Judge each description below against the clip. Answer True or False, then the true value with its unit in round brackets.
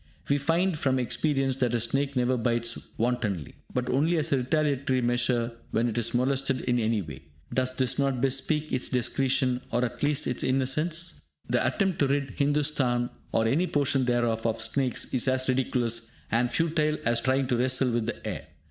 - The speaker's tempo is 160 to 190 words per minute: True (185 wpm)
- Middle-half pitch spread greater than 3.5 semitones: False (2.7 semitones)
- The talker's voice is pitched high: False (130 Hz)